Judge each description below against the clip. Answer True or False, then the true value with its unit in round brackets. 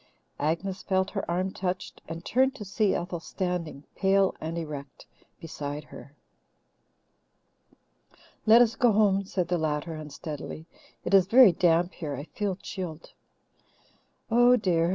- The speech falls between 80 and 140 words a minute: True (135 wpm)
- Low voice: False (180 Hz)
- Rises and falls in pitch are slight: False (3.6 semitones)